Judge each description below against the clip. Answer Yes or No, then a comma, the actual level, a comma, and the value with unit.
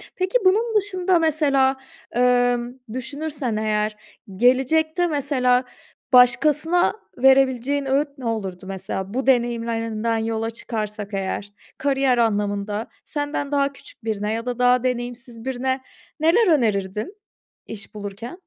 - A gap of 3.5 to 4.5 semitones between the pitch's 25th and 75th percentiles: Yes, average, 4.2 semitones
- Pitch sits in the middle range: No, very high, 250 Hz